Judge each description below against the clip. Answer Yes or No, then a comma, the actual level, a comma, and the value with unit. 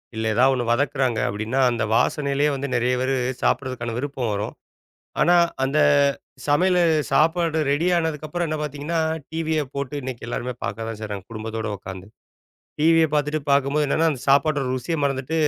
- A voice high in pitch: No, medium, 140 Hz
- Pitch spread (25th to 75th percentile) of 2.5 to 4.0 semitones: No, average, 4.5 semitones